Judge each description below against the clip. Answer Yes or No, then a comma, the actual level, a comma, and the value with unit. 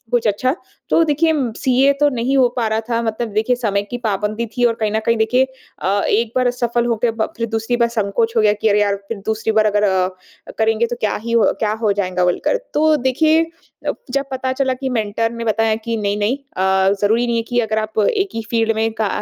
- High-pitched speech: Yes, high, 230 Hz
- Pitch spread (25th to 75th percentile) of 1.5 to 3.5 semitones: Yes, narrow, 2.5 semitones